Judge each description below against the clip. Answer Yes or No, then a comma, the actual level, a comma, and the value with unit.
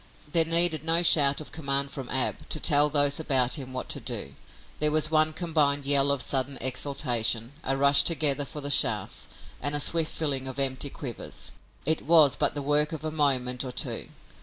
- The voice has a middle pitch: Yes, medium, 145 Hz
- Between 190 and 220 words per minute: Yes, average, 195 wpm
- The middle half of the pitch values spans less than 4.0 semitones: Yes, narrow, 2.4 semitones